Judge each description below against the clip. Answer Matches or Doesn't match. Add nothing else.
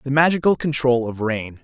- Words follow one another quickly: Doesn't match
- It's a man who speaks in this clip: Matches